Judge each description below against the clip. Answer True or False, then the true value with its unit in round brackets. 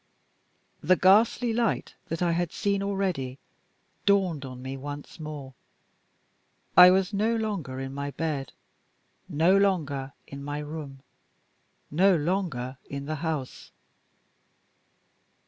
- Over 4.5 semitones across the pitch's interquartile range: True (5.5 semitones)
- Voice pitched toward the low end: False (160 Hz)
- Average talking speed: False (115 wpm)